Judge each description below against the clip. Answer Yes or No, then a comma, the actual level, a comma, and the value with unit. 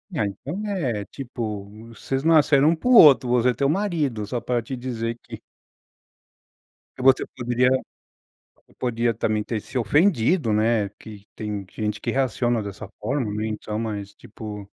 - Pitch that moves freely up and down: No, average, 4.1 semitones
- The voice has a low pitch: Yes, low, 120 Hz